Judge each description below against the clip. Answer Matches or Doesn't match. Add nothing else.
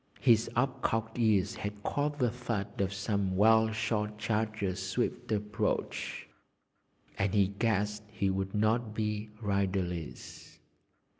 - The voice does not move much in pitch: Matches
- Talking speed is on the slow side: Matches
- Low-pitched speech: Matches